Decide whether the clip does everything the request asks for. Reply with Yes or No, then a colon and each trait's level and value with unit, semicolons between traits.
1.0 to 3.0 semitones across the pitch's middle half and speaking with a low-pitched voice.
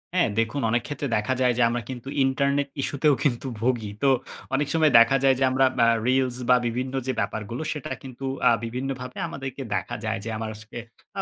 Yes: narrow, 2.6 semitones; low, 130 Hz